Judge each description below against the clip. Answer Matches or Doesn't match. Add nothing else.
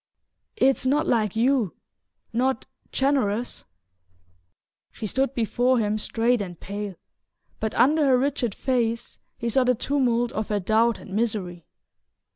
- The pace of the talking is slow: Matches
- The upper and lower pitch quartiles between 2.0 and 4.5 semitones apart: Matches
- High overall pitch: Matches